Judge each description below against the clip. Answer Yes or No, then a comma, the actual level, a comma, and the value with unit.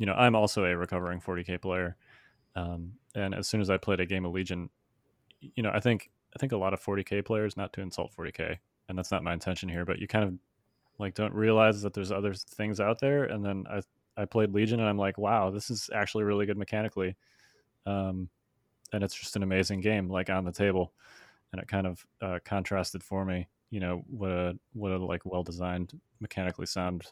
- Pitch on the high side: No, low, 100 Hz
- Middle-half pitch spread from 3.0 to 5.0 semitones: No, narrow, 2.6 semitones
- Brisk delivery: Yes, fast, 220 wpm